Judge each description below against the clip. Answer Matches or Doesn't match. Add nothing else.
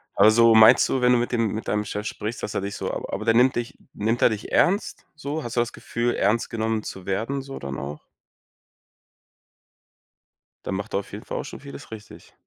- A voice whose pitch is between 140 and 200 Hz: Doesn't match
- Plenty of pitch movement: Doesn't match